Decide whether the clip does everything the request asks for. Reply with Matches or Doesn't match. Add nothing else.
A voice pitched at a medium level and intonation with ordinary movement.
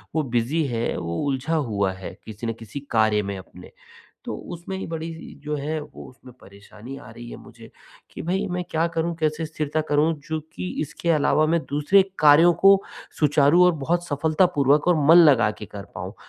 Doesn't match